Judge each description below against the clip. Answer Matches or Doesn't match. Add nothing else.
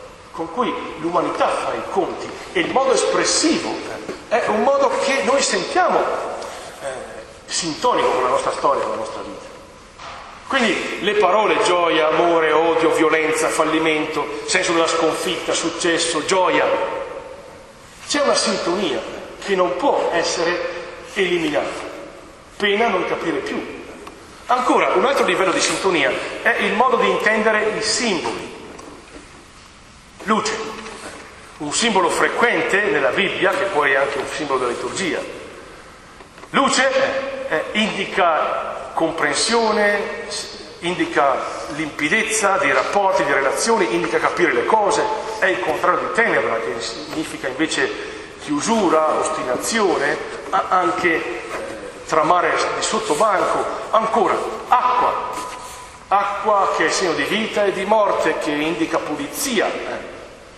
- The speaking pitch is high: Matches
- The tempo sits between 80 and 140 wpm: Matches